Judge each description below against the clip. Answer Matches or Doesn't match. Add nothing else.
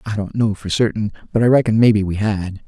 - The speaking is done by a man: Matches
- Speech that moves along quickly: Matches